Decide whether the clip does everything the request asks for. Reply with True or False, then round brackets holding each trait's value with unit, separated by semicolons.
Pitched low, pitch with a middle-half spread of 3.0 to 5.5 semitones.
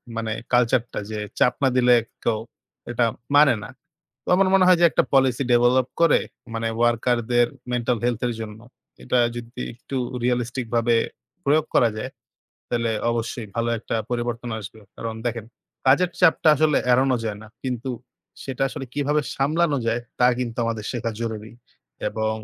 False (120 Hz; 2.4 semitones)